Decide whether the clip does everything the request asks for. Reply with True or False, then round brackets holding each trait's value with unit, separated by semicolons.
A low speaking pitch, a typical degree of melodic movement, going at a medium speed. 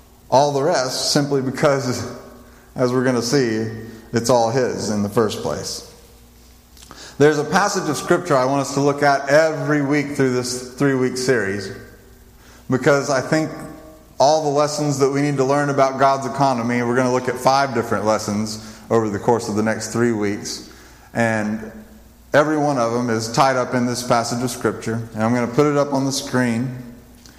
True (125 Hz; 3.8 semitones; 195 wpm)